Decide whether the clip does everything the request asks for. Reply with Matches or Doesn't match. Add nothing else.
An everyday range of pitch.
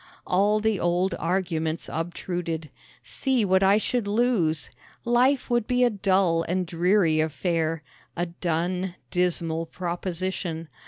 Matches